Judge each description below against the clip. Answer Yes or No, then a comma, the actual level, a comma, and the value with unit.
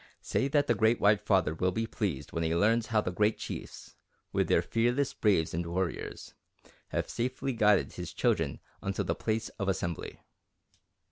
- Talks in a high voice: No, low, 105 Hz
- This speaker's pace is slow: No, average, 175 wpm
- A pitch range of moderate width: Yes, average, 4.0 semitones